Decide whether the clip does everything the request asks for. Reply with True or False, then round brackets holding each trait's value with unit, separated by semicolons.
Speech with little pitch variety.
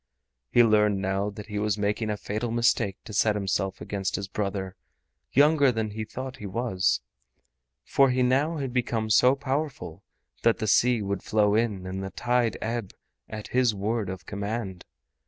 False (3.4 semitones)